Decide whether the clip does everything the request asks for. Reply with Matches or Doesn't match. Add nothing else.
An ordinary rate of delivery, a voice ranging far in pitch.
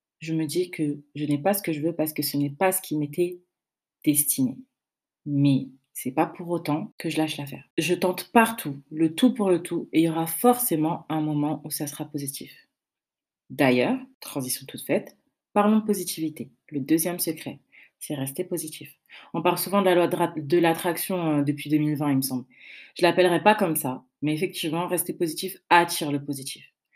Doesn't match